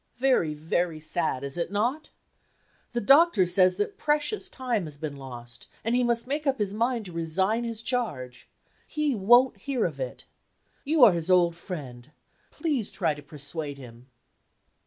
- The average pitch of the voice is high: Yes, high, 195 Hz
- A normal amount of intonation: No, wide, 8.3 semitones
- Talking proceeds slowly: No, average, 165 wpm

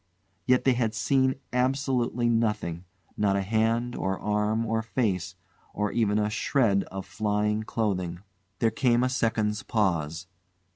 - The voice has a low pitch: Yes, low, 110 Hz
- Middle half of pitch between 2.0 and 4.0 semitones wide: Yes, average, 2.9 semitones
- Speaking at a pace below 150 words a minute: Yes, average, 140 wpm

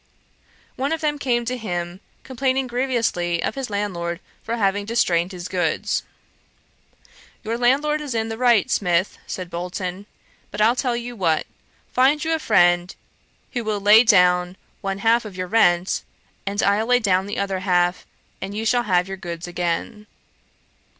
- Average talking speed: Yes, average, 165 wpm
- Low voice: No, high, 205 Hz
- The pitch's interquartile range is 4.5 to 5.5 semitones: Yes, average, 5.1 semitones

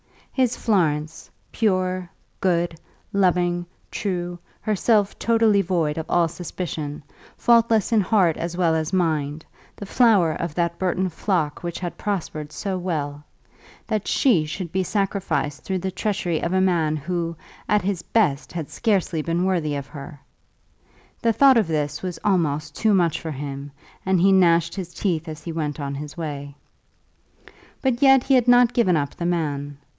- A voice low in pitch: No, medium, 175 Hz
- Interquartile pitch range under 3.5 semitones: No, average, 4.1 semitones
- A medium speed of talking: Yes, average, 160 wpm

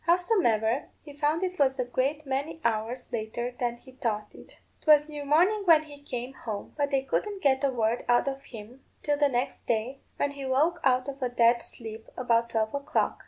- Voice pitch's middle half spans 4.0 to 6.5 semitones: No, average, 3.6 semitones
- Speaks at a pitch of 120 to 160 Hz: No, very high, 265 Hz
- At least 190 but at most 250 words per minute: Yes, fast, 205 wpm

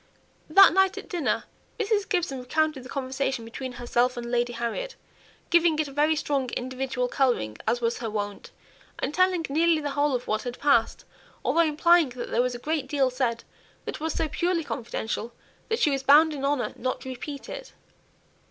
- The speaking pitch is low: No, very high, 275 Hz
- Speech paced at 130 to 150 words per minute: No, average, 190 wpm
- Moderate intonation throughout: Yes, average, 4.5 semitones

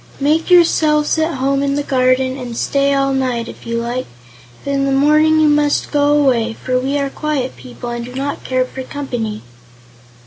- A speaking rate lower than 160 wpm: No, average, 195 wpm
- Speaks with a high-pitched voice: Yes, very high, 275 Hz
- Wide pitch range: No, narrow, 2.5 semitones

